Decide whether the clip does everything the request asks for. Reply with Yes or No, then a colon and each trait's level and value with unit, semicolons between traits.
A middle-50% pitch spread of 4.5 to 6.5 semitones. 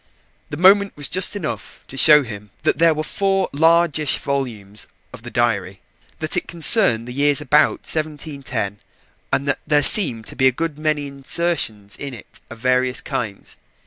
Yes: average, 4.9 semitones